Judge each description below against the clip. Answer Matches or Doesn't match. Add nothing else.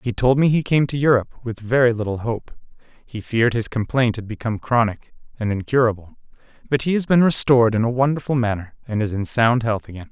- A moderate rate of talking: Doesn't match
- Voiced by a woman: Doesn't match